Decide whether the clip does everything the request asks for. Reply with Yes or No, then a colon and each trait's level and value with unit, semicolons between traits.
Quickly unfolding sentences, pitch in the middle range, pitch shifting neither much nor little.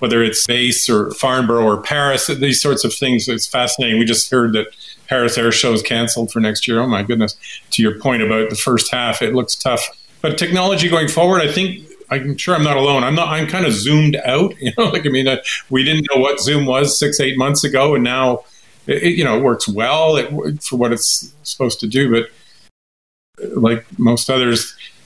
No: fast, 220 wpm; low, 130 Hz; average, 3.9 semitones